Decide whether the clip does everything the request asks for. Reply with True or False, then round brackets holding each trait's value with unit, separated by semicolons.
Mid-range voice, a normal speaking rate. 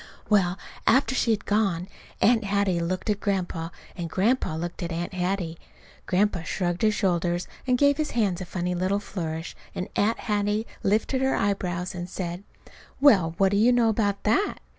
False (195 Hz; 175 wpm)